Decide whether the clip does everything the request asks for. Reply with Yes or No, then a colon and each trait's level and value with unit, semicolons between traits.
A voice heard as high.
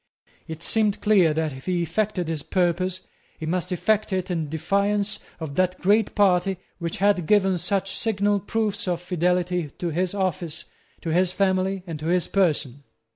No: medium, 180 Hz